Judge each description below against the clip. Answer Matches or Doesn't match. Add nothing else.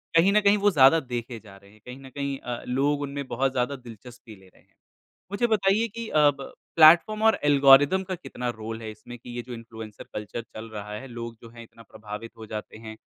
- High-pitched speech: Doesn't match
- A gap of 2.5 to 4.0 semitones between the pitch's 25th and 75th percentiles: Doesn't match